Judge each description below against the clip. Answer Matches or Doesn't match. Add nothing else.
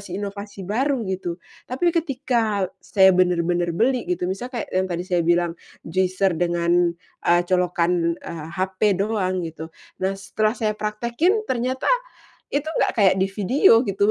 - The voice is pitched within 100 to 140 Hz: Doesn't match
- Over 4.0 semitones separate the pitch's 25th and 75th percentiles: Matches